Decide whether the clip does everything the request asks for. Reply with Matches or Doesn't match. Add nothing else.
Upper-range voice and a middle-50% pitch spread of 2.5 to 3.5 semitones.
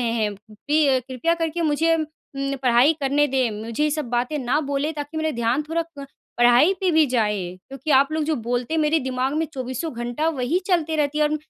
Doesn't match